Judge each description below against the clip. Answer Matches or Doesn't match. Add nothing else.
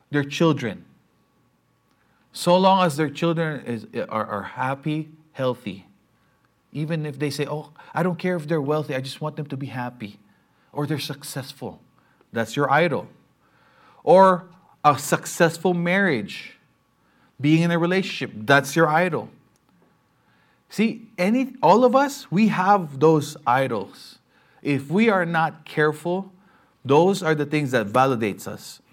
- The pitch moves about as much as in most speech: Matches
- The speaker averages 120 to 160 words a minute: Matches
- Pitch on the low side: Doesn't match